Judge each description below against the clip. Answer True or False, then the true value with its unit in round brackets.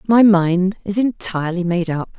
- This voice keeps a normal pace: True (165 wpm)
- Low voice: False (190 Hz)